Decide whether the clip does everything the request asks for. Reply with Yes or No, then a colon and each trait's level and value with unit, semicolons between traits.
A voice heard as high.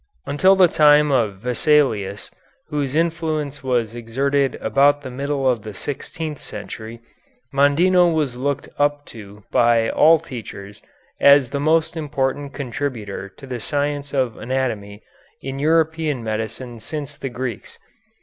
No: medium, 140 Hz